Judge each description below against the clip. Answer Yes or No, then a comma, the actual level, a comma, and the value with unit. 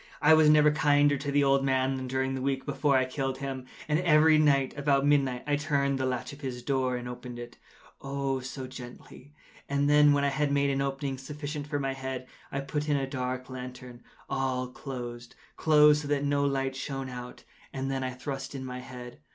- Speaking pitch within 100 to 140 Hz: Yes, low, 135 Hz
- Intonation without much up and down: Yes, narrow, 1.8 semitones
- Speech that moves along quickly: Yes, fast, 210 wpm